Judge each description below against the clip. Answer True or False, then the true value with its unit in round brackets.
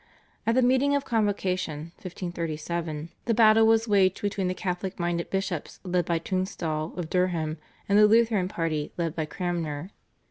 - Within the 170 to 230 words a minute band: False (155 wpm)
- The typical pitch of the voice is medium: True (180 Hz)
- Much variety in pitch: False (3.8 semitones)